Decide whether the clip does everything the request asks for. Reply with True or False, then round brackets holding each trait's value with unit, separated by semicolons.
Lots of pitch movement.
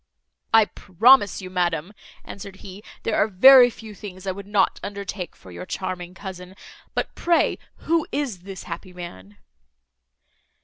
False (2.8 semitones)